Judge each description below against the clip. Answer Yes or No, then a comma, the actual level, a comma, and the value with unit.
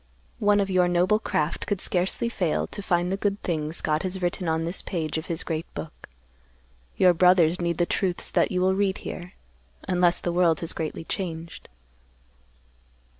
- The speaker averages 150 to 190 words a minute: Yes, average, 175 wpm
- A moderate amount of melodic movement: No, narrow, 2.3 semitones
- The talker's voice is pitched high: No, medium, 175 Hz